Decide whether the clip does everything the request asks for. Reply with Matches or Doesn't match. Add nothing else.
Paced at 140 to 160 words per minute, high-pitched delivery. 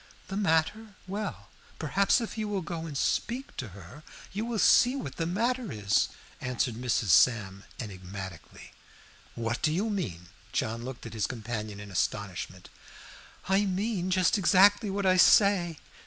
Doesn't match